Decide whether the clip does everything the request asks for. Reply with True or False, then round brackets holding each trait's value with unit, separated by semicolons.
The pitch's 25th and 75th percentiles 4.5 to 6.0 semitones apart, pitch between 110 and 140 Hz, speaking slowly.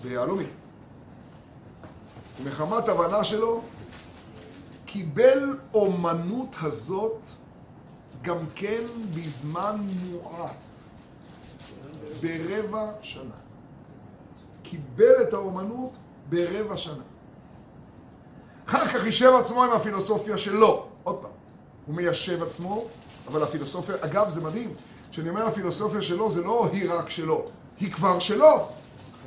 False (4.9 semitones; 190 Hz; 95 wpm)